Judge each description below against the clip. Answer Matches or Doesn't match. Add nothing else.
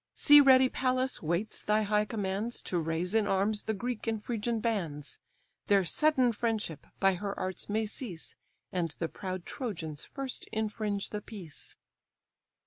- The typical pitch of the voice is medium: Doesn't match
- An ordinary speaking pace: Matches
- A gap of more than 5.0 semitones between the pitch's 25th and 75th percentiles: Doesn't match